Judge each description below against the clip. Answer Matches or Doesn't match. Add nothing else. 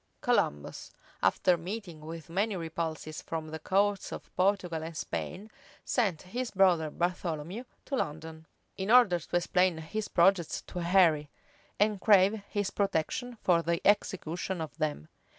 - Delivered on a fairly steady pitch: Doesn't match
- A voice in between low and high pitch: Matches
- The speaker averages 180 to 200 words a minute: Doesn't match